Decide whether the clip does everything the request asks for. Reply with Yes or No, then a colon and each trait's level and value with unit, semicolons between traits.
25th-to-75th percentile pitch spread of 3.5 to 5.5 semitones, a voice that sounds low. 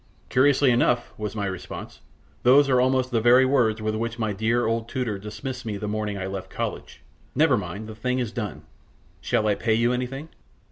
No: average, 2.9 semitones; low, 115 Hz